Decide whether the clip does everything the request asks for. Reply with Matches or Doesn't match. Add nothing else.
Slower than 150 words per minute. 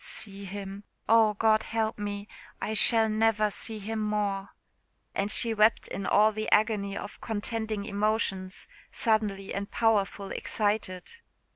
Matches